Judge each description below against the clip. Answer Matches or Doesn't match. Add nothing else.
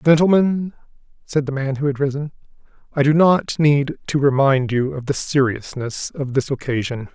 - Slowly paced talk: Doesn't match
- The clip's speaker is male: Matches